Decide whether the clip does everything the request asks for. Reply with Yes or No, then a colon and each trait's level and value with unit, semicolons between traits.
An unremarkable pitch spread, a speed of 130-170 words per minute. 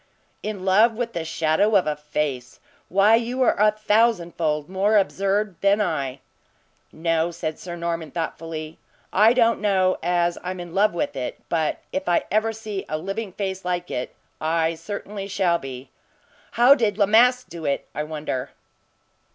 Yes: average, 4.6 semitones; average, 165 wpm